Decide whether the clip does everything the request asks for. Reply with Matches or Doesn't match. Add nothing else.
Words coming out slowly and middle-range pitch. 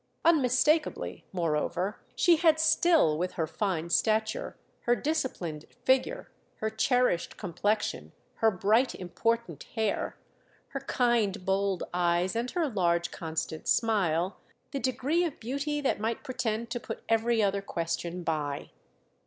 Doesn't match